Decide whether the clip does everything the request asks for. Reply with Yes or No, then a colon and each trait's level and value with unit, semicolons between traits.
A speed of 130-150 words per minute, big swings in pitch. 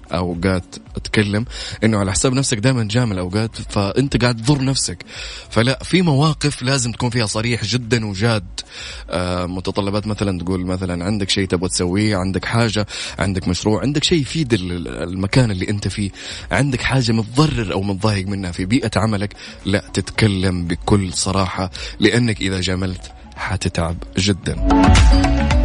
No: average, 140 wpm; average, 4.1 semitones